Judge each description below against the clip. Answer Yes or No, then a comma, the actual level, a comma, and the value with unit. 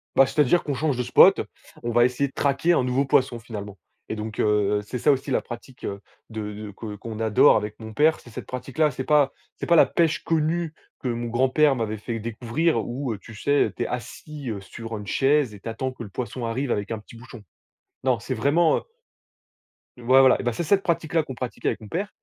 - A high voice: No, low, 125 Hz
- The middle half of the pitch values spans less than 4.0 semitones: No, average, 4.3 semitones